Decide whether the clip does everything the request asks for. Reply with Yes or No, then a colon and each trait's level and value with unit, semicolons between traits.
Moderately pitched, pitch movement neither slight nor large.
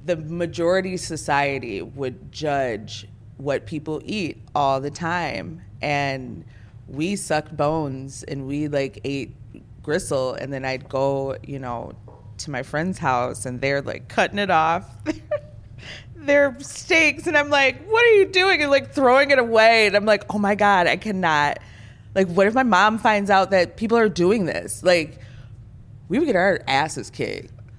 No: medium, 155 Hz; wide, 7.6 semitones